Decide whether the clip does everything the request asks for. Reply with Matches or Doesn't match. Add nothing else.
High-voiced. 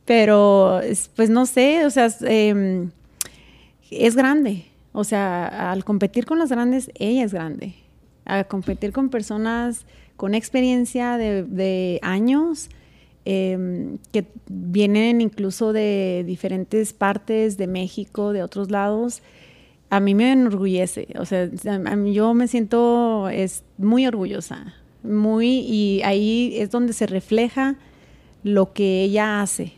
Matches